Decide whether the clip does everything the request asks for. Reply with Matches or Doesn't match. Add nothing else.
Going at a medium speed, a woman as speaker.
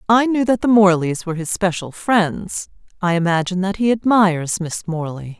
Matches